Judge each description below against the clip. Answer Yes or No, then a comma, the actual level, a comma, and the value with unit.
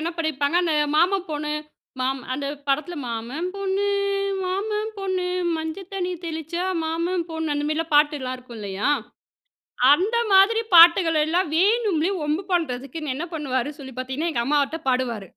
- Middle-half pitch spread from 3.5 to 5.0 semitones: Yes, average, 4.6 semitones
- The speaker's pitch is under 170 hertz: No, very high, 320 Hz